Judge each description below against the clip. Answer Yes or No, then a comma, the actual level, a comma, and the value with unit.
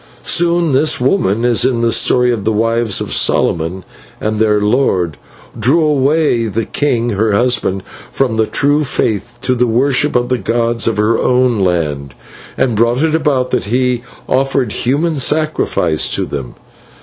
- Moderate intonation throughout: Yes, average, 4.0 semitones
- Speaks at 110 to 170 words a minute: Yes, average, 160 wpm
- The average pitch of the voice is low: Yes, low, 120 Hz